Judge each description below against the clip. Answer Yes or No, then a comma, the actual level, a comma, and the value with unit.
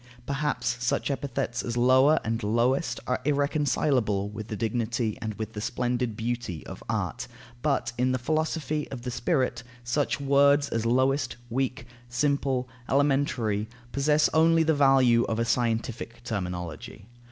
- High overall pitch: No, low, 125 Hz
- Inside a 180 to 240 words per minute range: No, average, 140 wpm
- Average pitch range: Yes, average, 3.5 semitones